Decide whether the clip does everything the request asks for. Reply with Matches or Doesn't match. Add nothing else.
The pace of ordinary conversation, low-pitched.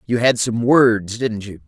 Doesn't match